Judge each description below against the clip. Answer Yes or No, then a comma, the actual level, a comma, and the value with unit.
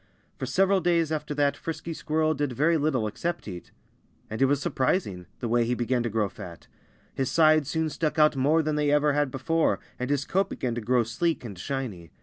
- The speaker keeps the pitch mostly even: No, average, 4.7 semitones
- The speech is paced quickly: Yes, fast, 210 wpm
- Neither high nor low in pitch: Yes, medium, 145 Hz